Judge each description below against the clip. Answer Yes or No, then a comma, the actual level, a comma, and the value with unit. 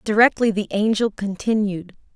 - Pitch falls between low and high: No, high, 210 Hz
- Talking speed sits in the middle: No, slow, 110 wpm